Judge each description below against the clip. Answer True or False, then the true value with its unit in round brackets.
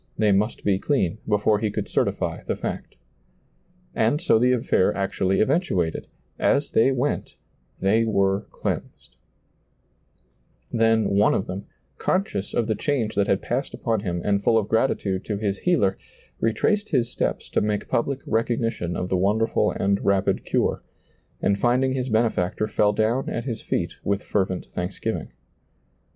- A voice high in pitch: False (110 Hz)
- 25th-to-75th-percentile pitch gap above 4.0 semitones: False (3.4 semitones)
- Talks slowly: False (155 wpm)